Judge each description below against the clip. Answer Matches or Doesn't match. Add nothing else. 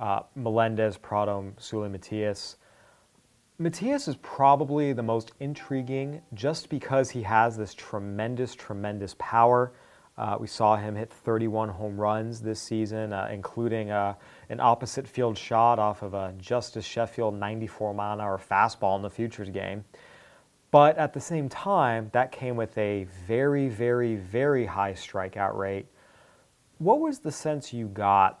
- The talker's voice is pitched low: Matches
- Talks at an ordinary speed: Matches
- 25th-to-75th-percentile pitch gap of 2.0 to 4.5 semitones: Matches